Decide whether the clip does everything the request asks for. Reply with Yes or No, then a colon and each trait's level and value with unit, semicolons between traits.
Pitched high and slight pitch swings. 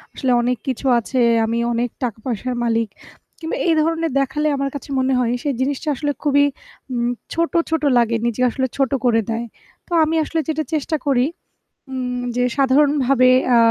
No: very high, 260 Hz; average, 3.4 semitones